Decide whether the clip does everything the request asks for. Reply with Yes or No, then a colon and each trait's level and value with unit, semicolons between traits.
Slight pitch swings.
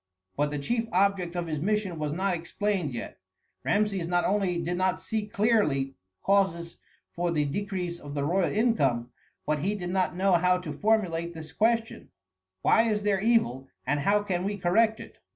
No: average, 4.0 semitones